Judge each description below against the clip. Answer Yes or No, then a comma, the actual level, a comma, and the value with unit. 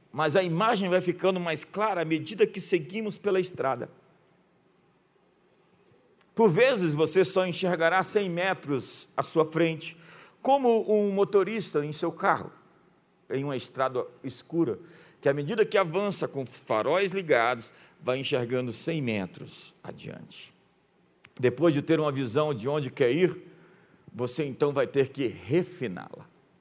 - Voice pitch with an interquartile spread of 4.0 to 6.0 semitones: Yes, average, 4.6 semitones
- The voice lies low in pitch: No, medium, 170 Hz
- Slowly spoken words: No, average, 140 wpm